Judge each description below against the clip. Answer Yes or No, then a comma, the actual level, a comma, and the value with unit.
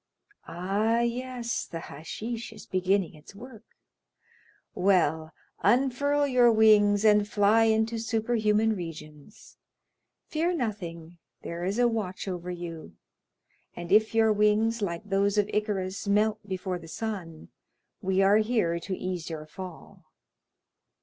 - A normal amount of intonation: Yes, average, 3.8 semitones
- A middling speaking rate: No, slow, 125 wpm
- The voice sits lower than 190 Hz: No, high, 205 Hz